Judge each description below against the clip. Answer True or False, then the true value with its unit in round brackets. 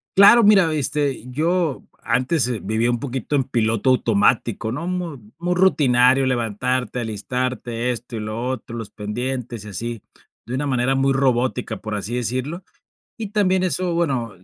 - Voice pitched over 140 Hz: False (125 Hz)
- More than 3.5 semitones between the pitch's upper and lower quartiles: True (4.2 semitones)